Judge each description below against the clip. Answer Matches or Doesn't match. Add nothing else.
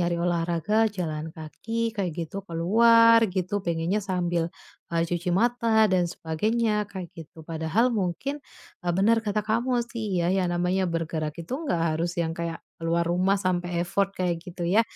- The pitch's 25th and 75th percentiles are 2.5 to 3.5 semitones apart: Doesn't match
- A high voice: Doesn't match